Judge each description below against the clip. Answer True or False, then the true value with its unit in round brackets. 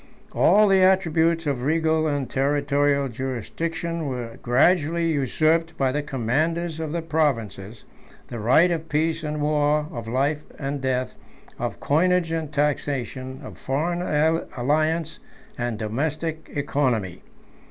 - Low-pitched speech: False (150 Hz)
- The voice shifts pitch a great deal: False (3.7 semitones)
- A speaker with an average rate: False (125 wpm)